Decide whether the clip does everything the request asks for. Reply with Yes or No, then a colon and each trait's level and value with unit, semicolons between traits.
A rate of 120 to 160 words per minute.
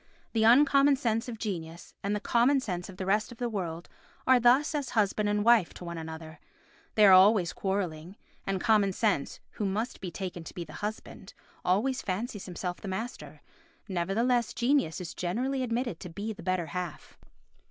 No: average, 180 wpm